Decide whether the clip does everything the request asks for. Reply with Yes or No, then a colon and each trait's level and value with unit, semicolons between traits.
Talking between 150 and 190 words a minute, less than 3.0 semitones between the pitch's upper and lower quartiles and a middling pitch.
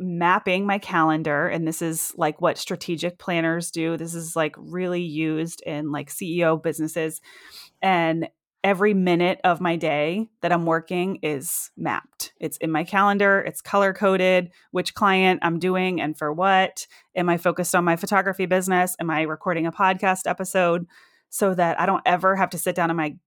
Yes: average, 180 wpm; narrow, 2.4 semitones; medium, 175 Hz